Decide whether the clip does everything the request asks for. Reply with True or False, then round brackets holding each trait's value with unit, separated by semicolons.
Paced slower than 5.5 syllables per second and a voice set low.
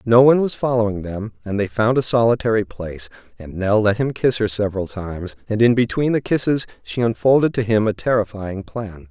False (5.6 syllables/s; 110 Hz)